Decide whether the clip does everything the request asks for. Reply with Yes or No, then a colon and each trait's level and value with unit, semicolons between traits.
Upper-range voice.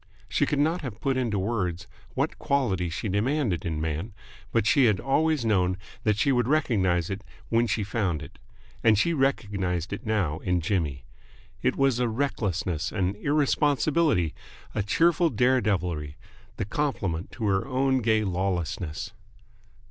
No: low, 105 Hz